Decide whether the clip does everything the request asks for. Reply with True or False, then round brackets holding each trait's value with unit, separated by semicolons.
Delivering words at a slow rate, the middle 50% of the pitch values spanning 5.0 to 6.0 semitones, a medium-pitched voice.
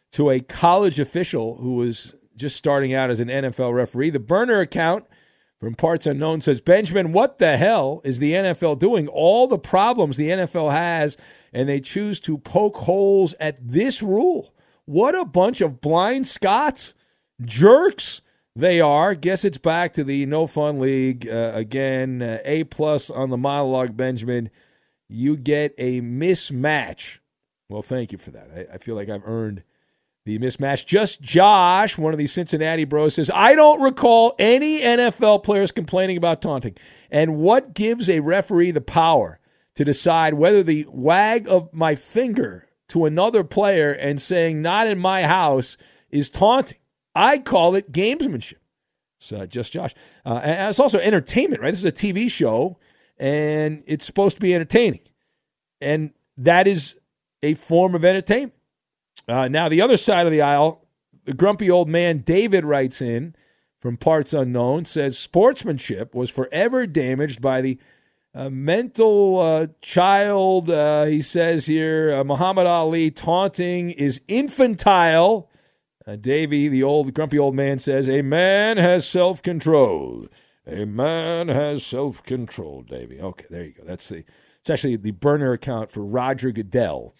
False (160 wpm; 5.6 semitones; 155 Hz)